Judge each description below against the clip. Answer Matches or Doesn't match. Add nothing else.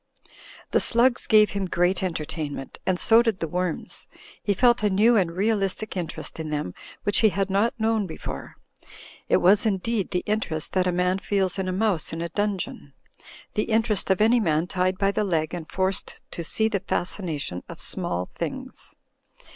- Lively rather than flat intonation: Doesn't match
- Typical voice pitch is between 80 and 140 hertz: Doesn't match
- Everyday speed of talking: Matches